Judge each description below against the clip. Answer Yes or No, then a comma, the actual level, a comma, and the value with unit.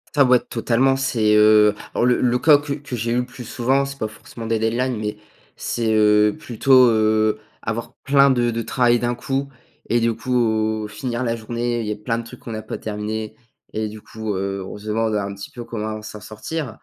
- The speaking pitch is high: No, low, 115 Hz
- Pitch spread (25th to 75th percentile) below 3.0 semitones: Yes, narrow, 2.5 semitones